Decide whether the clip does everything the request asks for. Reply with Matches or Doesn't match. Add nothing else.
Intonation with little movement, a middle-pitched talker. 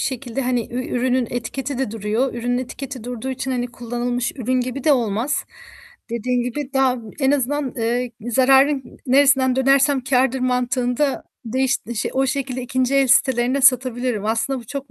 Doesn't match